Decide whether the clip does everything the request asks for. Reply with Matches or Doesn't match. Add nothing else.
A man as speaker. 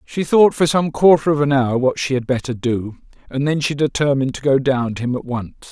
Matches